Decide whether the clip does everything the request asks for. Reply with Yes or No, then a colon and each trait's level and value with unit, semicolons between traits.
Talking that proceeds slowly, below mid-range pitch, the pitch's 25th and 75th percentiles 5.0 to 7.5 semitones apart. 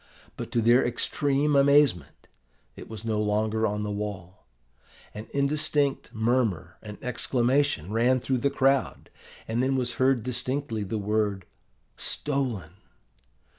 No: slow, 130 wpm; low, 120 Hz; average, 4.4 semitones